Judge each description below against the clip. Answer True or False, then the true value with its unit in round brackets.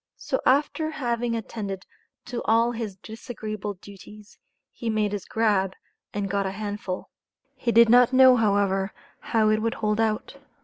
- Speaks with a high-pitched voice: True (215 Hz)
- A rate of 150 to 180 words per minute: True (160 wpm)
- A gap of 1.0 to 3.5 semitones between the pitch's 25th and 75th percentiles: True (2.6 semitones)